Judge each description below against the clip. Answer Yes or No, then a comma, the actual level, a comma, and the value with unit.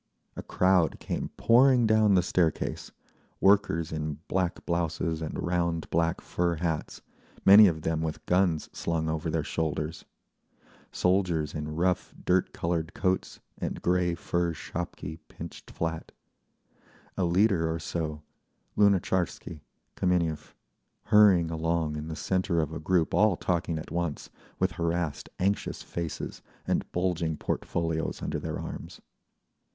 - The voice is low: Yes, very low, 85 Hz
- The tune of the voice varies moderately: No, narrow, 2.2 semitones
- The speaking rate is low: Yes, slow, 125 wpm